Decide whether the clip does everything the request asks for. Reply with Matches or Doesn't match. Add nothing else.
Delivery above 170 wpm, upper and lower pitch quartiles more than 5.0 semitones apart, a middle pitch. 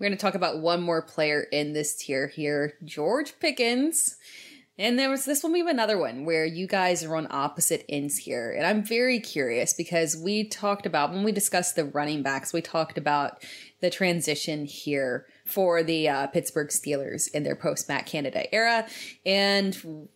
Matches